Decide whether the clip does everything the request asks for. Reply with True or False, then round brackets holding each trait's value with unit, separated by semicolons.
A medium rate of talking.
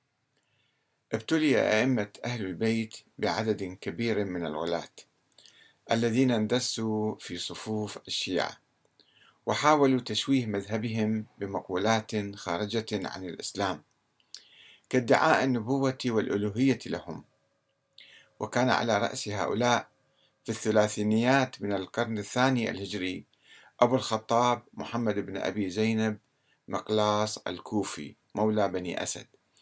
True (90 wpm)